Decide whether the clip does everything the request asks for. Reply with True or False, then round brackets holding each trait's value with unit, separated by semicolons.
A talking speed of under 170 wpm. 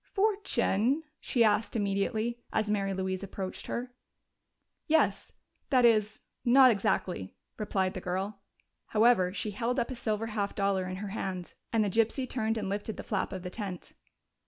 True (160 wpm)